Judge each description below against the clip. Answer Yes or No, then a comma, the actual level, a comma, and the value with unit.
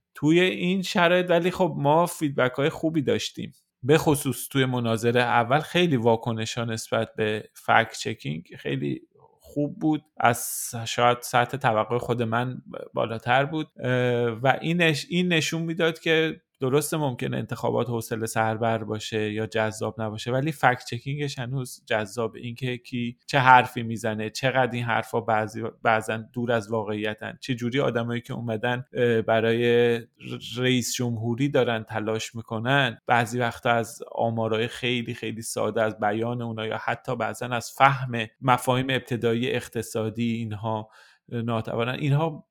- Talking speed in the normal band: Yes, average, 140 wpm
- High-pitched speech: No, low, 120 Hz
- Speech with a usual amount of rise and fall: Yes, average, 3.3 semitones